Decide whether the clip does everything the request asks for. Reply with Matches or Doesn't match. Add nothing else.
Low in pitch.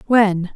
Doesn't match